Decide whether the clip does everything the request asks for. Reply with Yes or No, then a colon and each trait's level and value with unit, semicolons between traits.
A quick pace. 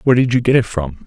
Yes: fast, 340 wpm